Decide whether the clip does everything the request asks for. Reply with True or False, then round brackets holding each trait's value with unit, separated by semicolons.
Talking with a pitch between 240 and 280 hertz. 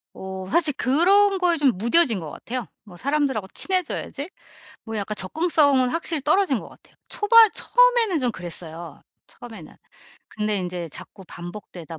True (255 Hz)